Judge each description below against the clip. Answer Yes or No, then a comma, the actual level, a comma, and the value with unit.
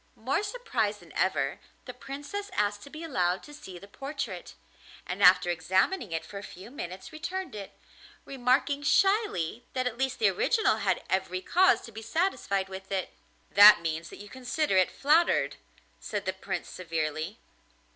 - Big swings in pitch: Yes, wide, 7.9 semitones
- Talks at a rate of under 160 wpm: No, average, 165 wpm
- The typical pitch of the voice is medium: No, high, 215 Hz